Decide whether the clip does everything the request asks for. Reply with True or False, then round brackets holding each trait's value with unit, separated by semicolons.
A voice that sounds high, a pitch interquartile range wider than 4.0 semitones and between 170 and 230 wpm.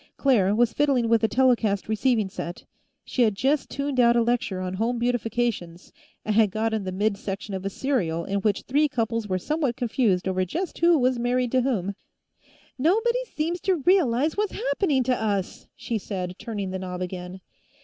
True (230 Hz; 5.1 semitones; 185 wpm)